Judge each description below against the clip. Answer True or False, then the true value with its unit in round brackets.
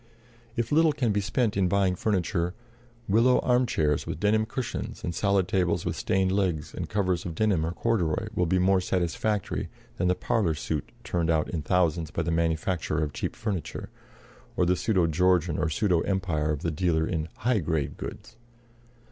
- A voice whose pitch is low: True (90 Hz)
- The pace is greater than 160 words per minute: True (180 wpm)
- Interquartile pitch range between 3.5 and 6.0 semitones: True (3.9 semitones)